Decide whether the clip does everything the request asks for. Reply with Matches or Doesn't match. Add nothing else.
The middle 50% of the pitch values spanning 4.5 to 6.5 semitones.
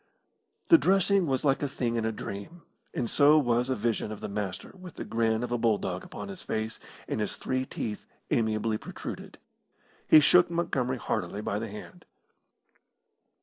Matches